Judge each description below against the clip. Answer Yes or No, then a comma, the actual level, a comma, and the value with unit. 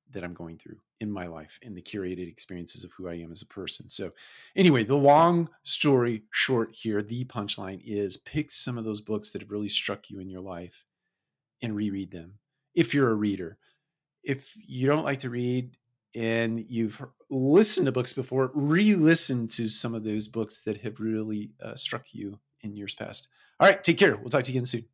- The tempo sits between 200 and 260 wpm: Yes, fast, 205 wpm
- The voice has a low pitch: Yes, low, 115 Hz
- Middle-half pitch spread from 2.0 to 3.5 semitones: No, average, 4.8 semitones